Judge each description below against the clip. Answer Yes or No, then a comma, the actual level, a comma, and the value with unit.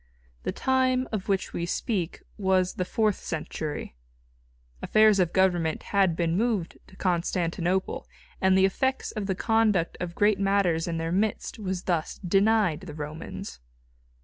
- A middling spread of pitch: Yes, average, 3.5 semitones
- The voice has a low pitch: No, high, 190 Hz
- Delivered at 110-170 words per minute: Yes, average, 150 wpm